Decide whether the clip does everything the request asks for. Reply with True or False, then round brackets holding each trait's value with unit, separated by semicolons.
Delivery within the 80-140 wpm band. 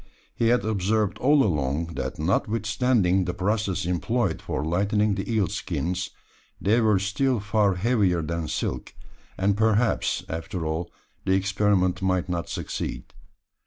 True (135 wpm)